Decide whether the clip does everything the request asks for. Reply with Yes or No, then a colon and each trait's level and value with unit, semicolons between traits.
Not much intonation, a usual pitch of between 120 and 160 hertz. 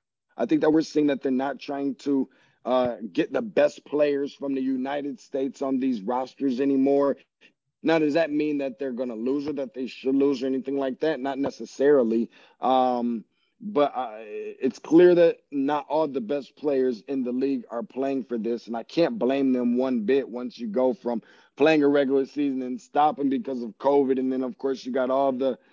Yes: narrow, 1.8 semitones; low, 135 Hz